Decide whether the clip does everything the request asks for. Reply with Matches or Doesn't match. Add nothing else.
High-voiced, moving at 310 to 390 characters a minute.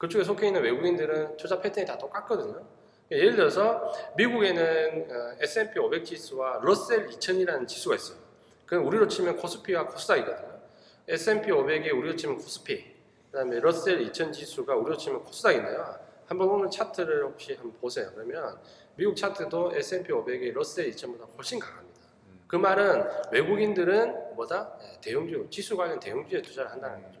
Matches